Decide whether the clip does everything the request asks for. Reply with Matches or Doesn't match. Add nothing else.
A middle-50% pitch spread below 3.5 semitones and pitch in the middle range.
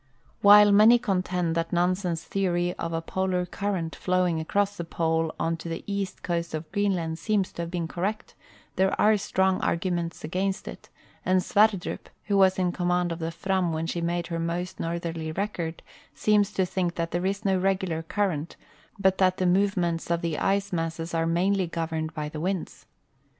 Matches